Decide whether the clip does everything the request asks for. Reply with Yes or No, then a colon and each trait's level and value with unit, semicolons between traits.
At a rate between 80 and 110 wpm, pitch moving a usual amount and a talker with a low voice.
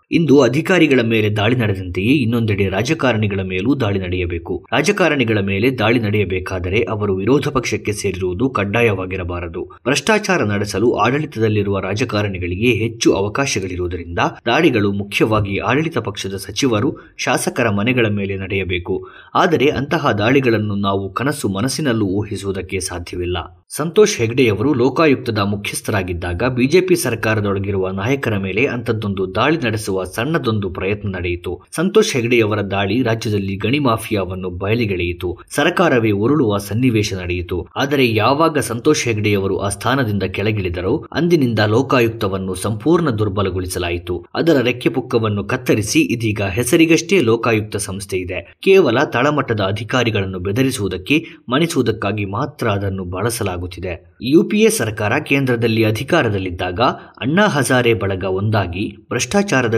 Yes: fast, 105 wpm; average, 4.9 semitones; low, 110 Hz